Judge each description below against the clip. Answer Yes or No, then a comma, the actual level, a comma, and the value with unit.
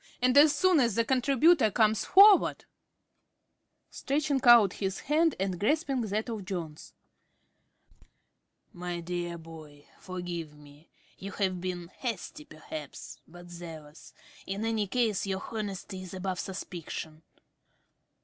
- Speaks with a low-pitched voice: No, high, 195 Hz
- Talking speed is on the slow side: Yes, slow, 125 wpm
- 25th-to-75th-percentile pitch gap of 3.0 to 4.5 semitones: No, wide, 5.6 semitones